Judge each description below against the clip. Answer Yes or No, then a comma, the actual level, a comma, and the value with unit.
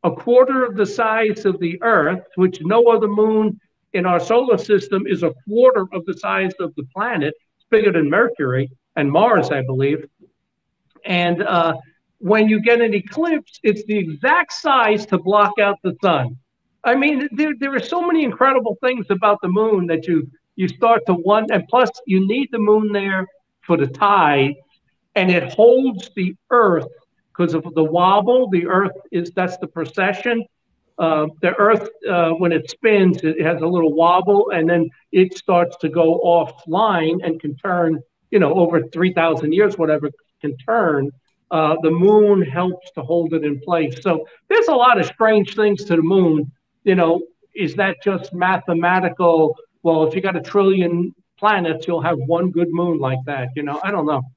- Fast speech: No, average, 185 wpm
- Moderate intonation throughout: Yes, average, 4.4 semitones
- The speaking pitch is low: No, medium, 185 Hz